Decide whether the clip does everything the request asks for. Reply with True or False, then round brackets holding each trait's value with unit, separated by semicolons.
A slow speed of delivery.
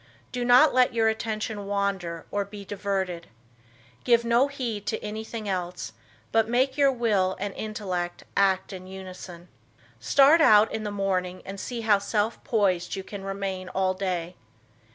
False (155 wpm)